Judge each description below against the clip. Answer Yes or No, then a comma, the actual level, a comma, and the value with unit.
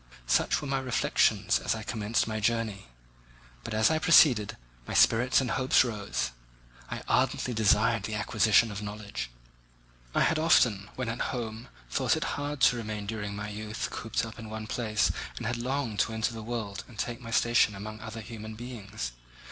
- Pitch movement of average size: No, narrow, 2.2 semitones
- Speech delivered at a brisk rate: No, average, 180 wpm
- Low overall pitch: Yes, low, 110 Hz